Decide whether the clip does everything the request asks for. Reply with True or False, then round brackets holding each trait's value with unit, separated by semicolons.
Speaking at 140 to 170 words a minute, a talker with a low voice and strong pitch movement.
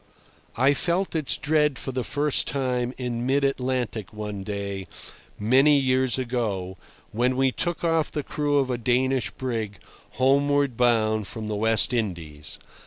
False (150 wpm; 125 Hz; 4.2 semitones)